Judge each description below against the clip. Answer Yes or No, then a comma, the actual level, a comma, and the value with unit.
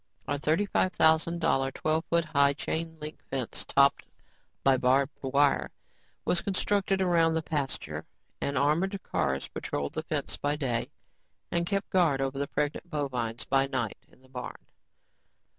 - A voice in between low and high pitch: Yes, medium, 145 Hz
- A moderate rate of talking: Yes, average, 155 wpm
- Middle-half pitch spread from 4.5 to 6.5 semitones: No, average, 3.7 semitones